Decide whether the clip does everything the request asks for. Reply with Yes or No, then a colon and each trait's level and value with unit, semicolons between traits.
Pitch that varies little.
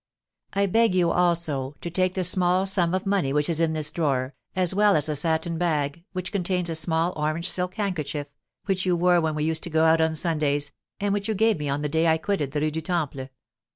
No: average, 3.3 semitones